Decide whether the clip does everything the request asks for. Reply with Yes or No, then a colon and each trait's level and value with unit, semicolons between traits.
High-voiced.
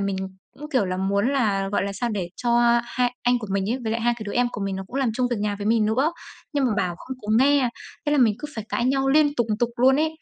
Yes: high, 240 Hz